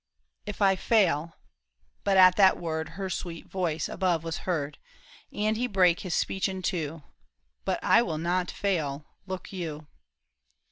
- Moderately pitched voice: Yes, medium, 175 Hz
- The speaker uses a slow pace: No, average, 170 wpm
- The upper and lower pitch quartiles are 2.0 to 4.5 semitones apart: Yes, average, 3.3 semitones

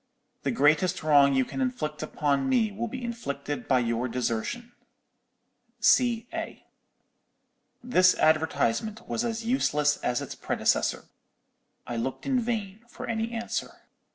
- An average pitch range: No, wide, 8.9 semitones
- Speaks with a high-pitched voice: Yes, high, 195 Hz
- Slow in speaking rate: Yes, slow, 130 wpm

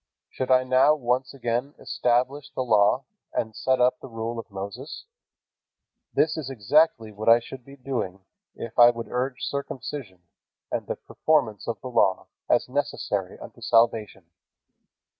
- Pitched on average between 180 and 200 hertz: No, low, 125 Hz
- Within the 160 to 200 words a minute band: No, average, 150 wpm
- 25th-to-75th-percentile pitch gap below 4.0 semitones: Yes, average, 3.1 semitones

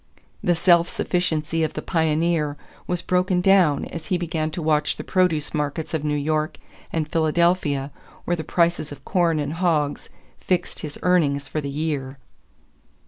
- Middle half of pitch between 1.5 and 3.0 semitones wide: Yes, average, 2.7 semitones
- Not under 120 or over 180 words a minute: Yes, average, 160 wpm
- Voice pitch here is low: No, medium, 160 Hz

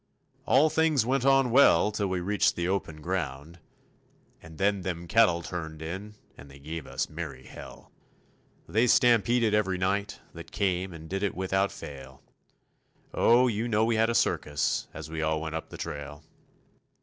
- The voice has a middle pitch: No, very low, 95 Hz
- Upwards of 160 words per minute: Yes, average, 170 wpm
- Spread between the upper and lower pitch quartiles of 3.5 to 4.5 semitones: No, wide, 5.6 semitones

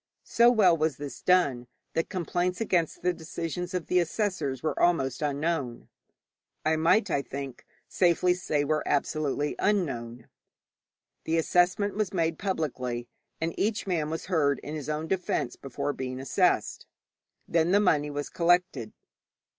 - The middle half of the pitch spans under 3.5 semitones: No, average, 4.1 semitones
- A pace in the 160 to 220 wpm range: No, average, 145 wpm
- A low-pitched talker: No, medium, 160 Hz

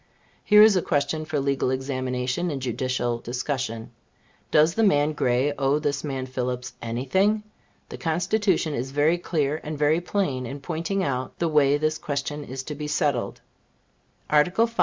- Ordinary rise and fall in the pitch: Yes, average, 3.5 semitones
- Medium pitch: Yes, medium, 145 Hz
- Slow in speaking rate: No, average, 165 wpm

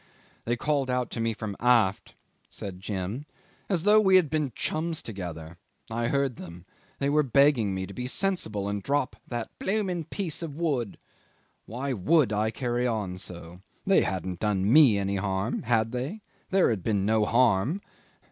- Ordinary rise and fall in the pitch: No, wide, 6.6 semitones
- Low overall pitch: Yes, low, 120 Hz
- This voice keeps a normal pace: Yes, average, 170 wpm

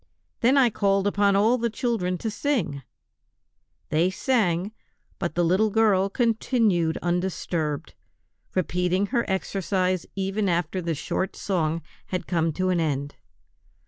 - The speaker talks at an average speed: No, slow, 130 wpm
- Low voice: No, high, 190 Hz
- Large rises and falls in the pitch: No, average, 3.6 semitones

